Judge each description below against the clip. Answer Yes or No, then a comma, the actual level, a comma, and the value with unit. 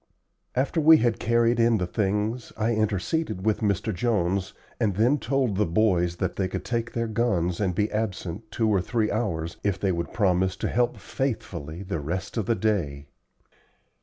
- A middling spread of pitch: Yes, average, 4.1 semitones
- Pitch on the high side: No, low, 105 Hz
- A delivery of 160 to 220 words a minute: Yes, average, 180 wpm